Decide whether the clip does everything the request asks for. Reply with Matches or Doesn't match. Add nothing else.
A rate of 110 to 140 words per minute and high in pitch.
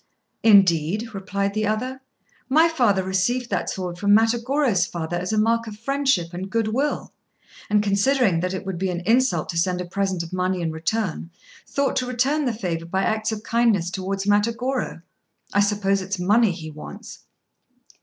Doesn't match